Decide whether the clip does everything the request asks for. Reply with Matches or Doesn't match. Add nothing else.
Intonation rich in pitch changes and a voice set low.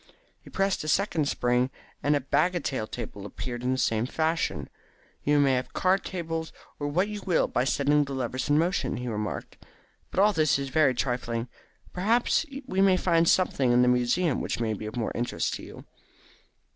Doesn't match